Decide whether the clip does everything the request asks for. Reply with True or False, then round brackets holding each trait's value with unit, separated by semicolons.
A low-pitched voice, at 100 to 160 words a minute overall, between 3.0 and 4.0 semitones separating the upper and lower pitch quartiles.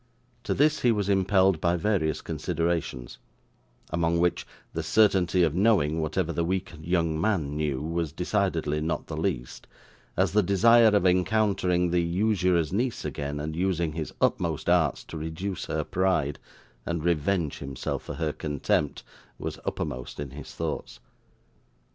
True (85 Hz; 150 wpm; 3.6 semitones)